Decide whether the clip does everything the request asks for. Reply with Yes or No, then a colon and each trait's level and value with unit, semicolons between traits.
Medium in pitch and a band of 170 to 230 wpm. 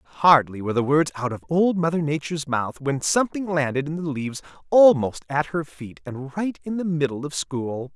Yes: medium, 150 Hz; fast, 205 wpm